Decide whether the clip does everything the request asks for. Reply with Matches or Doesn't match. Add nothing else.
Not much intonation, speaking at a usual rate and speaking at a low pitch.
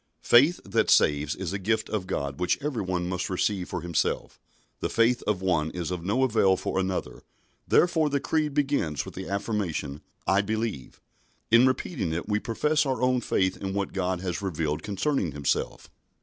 Doesn't match